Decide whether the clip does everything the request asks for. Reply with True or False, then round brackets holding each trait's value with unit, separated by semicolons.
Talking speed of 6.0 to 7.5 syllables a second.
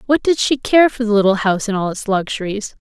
True (6.1 syllables/s)